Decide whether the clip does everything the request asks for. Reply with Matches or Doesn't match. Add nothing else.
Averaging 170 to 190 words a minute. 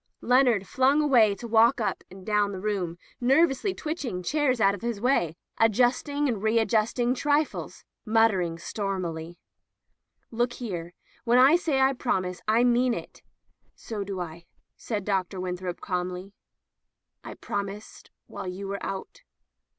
Doesn't match